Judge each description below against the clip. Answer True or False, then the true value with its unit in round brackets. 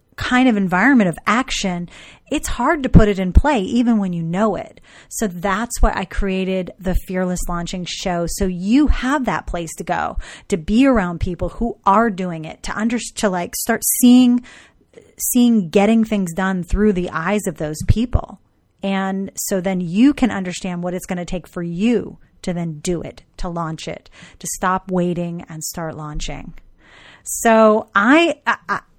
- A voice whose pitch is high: True (195 Hz)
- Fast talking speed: False (180 wpm)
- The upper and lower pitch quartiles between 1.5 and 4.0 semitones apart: False (4.5 semitones)